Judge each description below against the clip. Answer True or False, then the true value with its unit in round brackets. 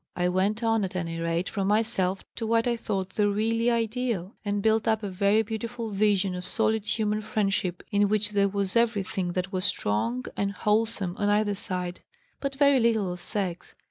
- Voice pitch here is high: True (205 Hz)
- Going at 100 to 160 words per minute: False (190 wpm)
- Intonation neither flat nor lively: True (3.0 semitones)